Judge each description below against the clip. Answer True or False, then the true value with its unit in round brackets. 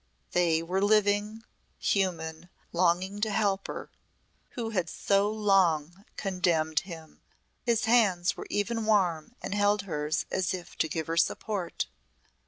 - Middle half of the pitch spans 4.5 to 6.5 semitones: False (3.5 semitones)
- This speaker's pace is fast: False (135 wpm)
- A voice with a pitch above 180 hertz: True (190 Hz)